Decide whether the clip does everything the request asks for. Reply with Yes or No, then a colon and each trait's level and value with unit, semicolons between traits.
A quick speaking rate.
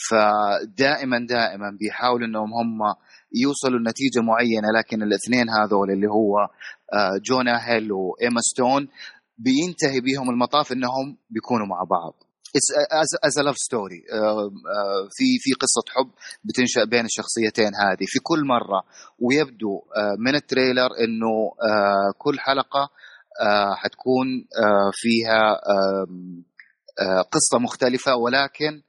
No: average, 105 wpm